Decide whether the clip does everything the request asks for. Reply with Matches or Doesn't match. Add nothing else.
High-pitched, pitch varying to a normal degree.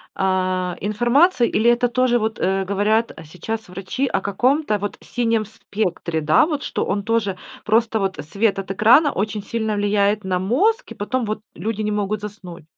Matches